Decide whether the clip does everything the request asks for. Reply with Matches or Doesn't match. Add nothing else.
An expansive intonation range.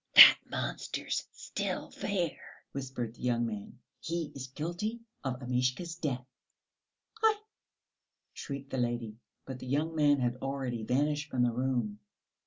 Doesn't match